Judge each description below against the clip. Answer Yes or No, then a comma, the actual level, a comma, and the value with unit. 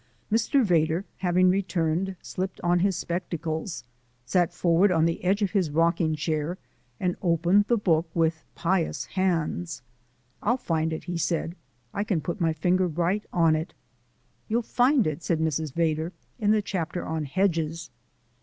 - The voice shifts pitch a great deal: No, average, 2.8 semitones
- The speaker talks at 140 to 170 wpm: Yes, average, 155 wpm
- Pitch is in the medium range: Yes, medium, 175 Hz